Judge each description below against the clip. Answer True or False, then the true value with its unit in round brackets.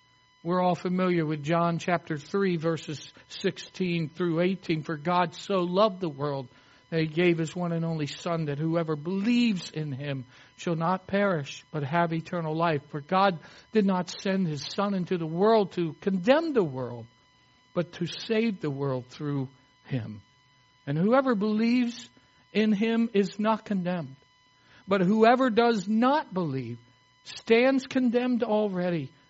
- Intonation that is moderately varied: False (5.8 semitones)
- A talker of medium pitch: True (170 Hz)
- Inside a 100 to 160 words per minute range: True (150 wpm)